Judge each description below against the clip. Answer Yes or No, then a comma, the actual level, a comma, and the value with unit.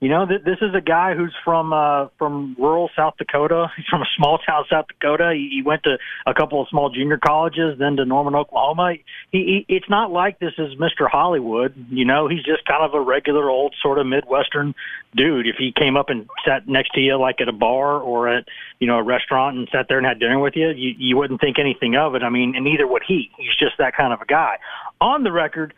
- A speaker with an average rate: No, fast, 245 wpm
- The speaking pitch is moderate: Yes, medium, 145 Hz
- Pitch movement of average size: Yes, average, 3.3 semitones